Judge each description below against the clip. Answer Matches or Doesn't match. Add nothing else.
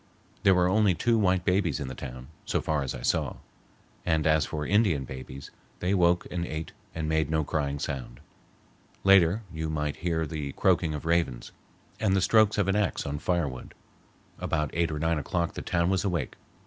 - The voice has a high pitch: Doesn't match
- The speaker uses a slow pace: Doesn't match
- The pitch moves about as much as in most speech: Matches